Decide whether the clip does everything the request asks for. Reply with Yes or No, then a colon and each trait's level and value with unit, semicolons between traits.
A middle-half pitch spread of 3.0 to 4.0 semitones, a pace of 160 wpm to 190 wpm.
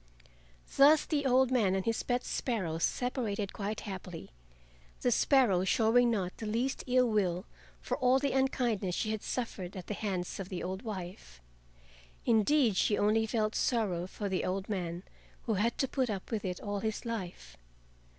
No: average, 4.6 semitones; average, 170 wpm